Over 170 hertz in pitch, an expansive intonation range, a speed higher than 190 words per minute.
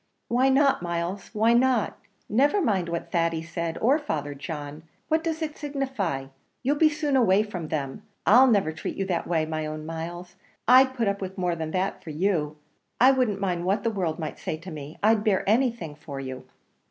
Yes: high, 190 Hz; wide, 7.4 semitones; average, 200 wpm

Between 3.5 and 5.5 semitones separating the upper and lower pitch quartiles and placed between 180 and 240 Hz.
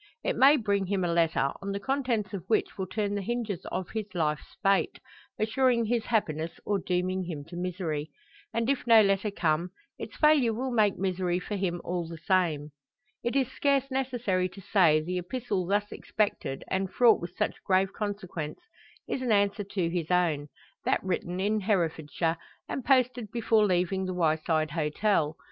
Yes: average, 4.2 semitones; high, 190 Hz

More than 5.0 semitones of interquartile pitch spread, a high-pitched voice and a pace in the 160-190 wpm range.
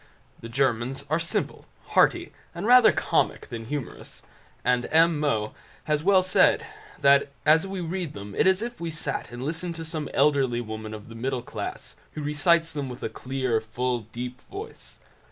No: wide, 5.4 semitones; medium, 140 Hz; average, 180 wpm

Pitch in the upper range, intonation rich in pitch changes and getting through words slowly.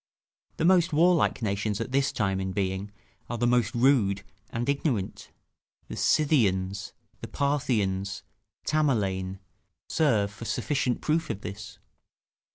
No: low, 115 Hz; wide, 6.2 semitones; slow, 125 wpm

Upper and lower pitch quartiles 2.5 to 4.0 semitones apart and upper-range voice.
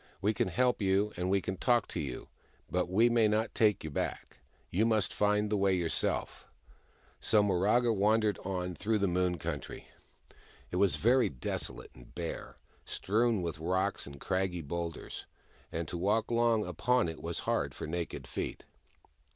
No: average, 3.7 semitones; very low, 95 Hz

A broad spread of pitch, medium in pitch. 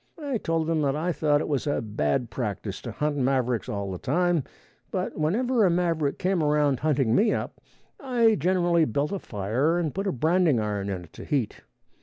Yes: wide, 6.1 semitones; medium, 150 Hz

